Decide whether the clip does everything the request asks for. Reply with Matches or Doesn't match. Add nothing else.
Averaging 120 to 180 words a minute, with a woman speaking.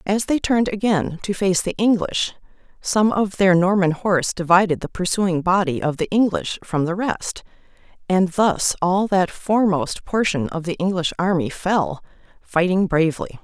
Matches